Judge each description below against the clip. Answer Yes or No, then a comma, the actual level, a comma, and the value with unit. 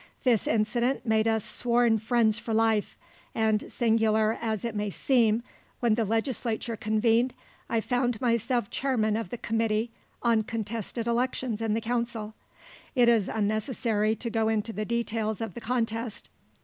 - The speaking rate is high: No, average, 150 wpm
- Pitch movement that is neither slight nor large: No, narrow, 1.6 semitones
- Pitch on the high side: Yes, high, 225 Hz